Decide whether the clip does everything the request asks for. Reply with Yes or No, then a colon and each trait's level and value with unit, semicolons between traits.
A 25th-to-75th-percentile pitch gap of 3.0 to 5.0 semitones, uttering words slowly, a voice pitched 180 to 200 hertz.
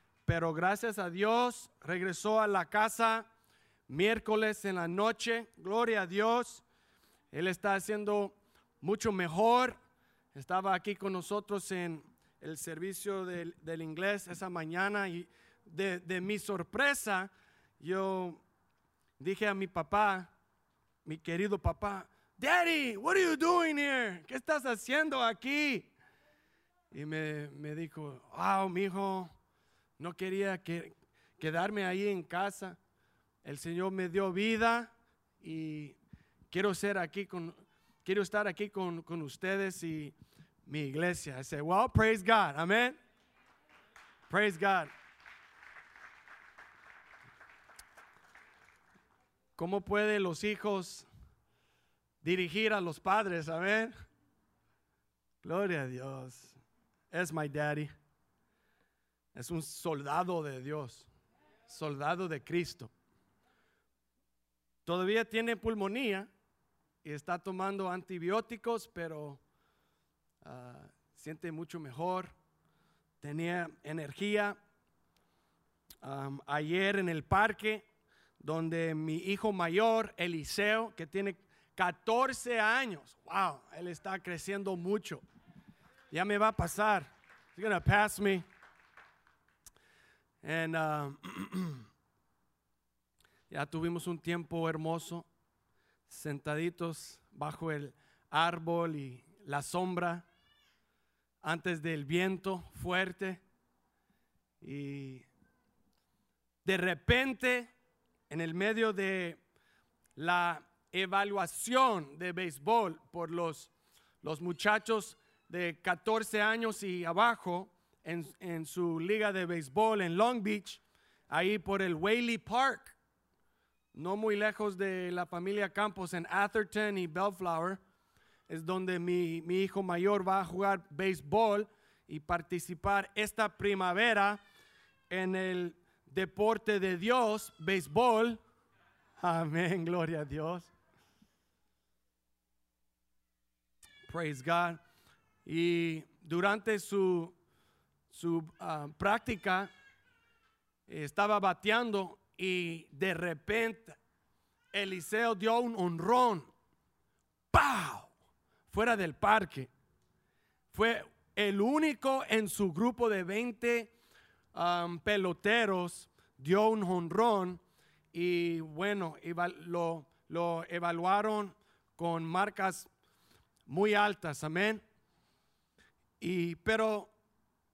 Yes: average, 4.0 semitones; slow, 100 wpm; medium, 185 Hz